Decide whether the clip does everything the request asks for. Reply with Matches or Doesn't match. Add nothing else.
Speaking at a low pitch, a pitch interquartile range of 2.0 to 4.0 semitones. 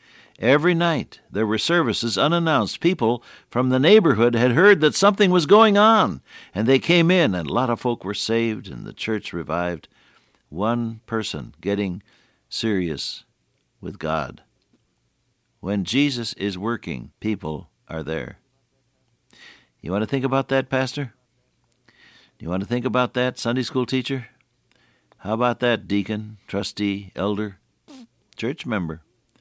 Doesn't match